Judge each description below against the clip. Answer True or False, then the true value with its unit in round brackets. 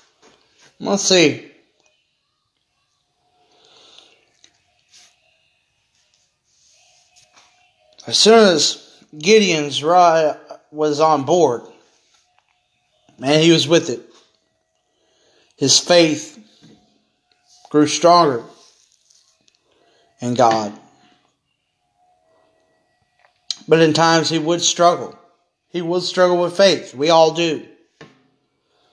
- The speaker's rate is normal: False (75 wpm)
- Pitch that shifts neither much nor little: True (3.1 semitones)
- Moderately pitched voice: True (165 Hz)